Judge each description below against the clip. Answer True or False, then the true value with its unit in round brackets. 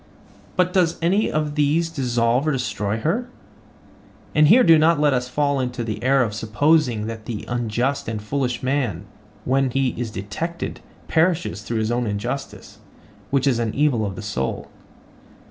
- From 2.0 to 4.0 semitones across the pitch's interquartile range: False (5.2 semitones)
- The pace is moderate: True (160 wpm)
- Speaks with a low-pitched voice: True (130 Hz)